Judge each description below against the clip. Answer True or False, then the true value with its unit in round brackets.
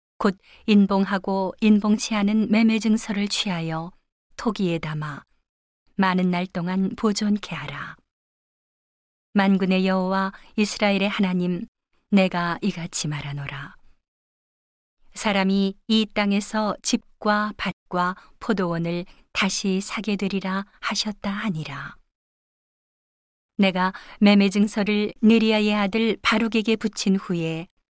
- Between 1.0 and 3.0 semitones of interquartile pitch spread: True (2.7 semitones)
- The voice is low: False (200 Hz)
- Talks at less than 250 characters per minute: True (225 characters per minute)